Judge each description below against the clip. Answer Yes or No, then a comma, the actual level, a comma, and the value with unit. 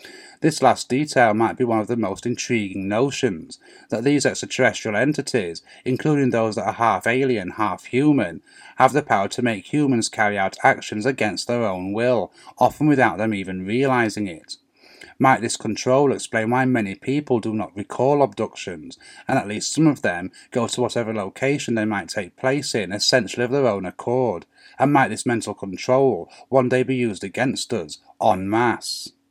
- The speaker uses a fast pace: No, average, 175 wpm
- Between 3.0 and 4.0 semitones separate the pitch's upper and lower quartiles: Yes, average, 3.7 semitones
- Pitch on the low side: Yes, low, 120 Hz